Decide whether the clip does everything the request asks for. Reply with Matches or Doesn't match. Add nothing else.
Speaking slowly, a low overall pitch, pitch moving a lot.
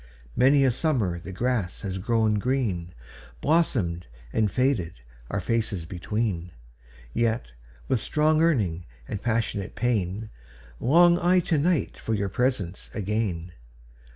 Matches